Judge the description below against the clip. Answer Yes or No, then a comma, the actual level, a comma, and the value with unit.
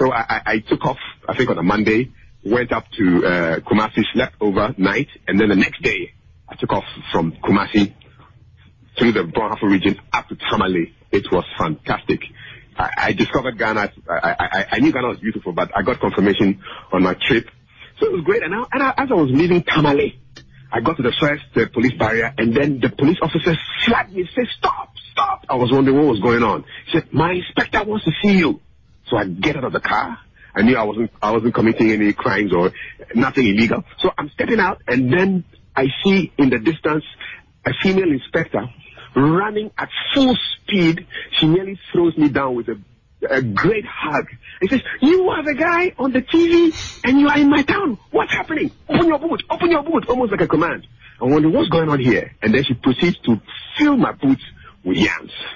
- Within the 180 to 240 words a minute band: Yes, fast, 205 wpm